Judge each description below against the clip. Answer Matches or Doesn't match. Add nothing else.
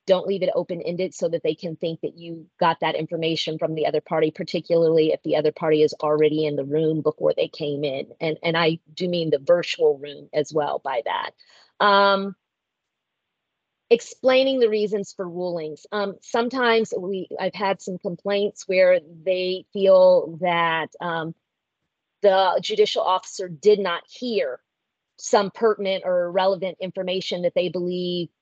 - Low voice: Doesn't match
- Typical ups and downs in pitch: Matches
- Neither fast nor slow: Matches